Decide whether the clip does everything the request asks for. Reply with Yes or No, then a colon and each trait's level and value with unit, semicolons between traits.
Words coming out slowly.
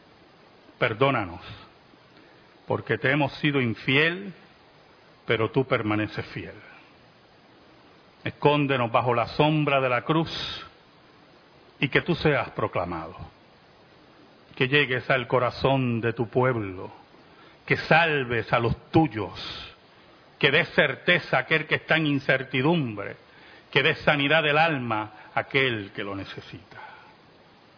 Yes: slow, 115 wpm